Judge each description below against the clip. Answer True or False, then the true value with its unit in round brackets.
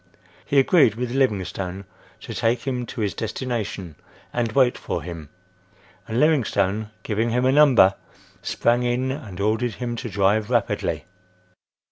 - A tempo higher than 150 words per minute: False (140 wpm)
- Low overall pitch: True (115 Hz)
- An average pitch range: True (3.8 semitones)